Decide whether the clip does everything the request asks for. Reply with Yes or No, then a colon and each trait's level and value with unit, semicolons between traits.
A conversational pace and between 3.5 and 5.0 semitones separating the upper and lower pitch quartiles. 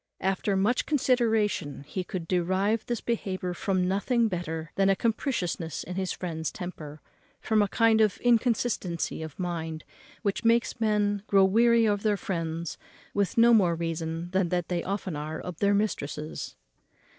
Yes: average, 155 wpm; average, 4.3 semitones